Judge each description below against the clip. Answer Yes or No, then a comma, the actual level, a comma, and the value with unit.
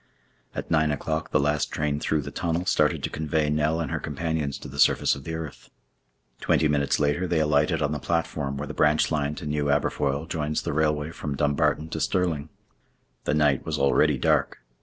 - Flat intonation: Yes, narrow, 1.5 semitones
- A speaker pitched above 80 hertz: No, very low, 75 Hz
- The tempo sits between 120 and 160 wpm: No, average, 200 wpm